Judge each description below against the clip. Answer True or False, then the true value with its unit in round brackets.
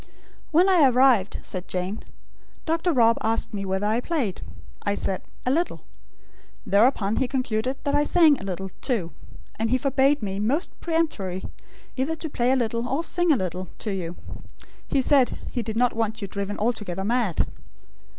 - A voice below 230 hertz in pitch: False (235 Hz)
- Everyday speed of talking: True (170 wpm)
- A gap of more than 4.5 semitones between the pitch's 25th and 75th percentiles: True (5.6 semitones)